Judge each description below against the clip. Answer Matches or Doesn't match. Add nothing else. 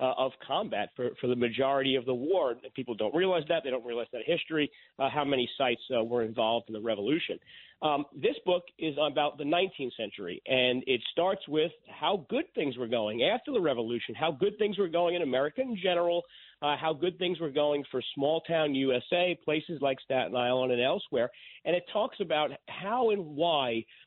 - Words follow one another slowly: Doesn't match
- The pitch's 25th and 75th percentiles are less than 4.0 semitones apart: Doesn't match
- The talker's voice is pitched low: Doesn't match